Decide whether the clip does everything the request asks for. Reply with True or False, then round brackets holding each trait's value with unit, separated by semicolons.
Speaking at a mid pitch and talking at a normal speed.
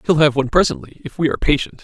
False (150 Hz; 260 wpm)